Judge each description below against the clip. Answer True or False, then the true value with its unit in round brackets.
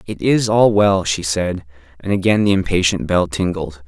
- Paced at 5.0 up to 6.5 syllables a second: False (4.7 syllables/s)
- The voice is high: False (90 Hz)